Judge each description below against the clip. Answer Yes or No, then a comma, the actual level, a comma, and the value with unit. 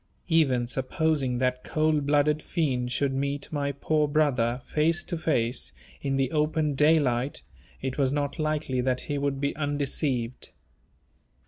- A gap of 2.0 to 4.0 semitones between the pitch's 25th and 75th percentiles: Yes, average, 2.9 semitones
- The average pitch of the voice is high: No, medium, 140 Hz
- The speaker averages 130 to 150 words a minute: Yes, average, 140 wpm